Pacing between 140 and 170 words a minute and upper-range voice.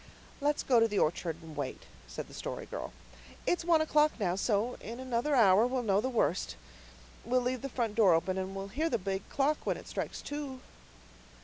No: fast, 205 wpm; high, 235 Hz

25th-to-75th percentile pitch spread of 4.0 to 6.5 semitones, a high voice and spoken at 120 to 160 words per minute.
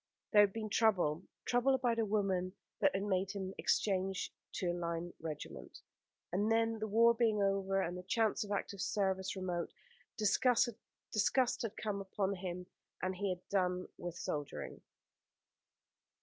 No: average, 2.9 semitones; high, 195 Hz; average, 150 wpm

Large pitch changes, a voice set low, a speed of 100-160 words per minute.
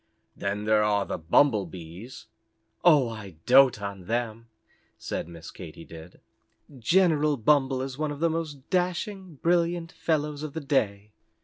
Yes: wide, 7.3 semitones; low, 130 Hz; average, 145 wpm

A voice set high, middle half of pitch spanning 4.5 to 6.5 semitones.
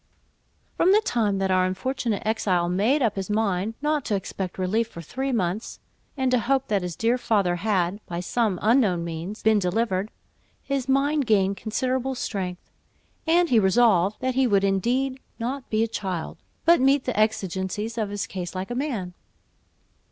Yes: high, 215 Hz; average, 5.1 semitones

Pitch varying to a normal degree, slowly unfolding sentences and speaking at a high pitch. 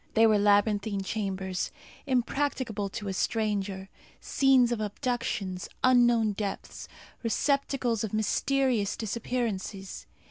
Yes: average, 3.3 semitones; slow, 100 wpm; high, 220 Hz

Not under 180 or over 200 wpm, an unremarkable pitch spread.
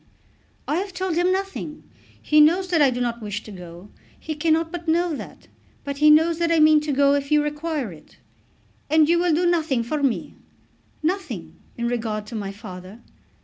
No: average, 195 wpm; wide, 6.0 semitones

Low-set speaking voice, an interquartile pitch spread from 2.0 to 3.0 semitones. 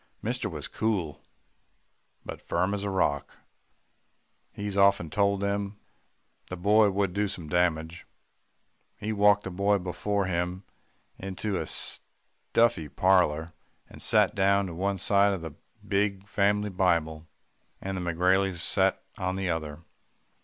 Yes: very low, 95 Hz; narrow, 2.5 semitones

